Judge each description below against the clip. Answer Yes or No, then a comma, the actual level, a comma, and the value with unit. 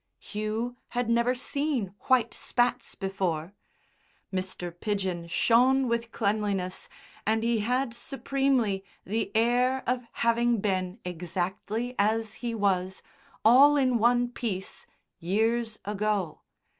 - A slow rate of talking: Yes, slow, 110 wpm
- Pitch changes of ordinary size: Yes, average, 4.0 semitones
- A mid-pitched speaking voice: No, high, 225 Hz